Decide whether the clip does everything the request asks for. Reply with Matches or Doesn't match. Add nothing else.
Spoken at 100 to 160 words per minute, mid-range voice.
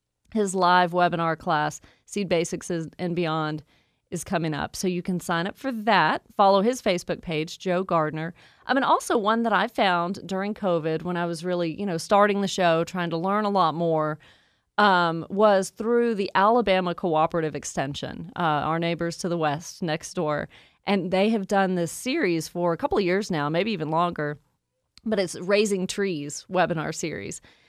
Doesn't match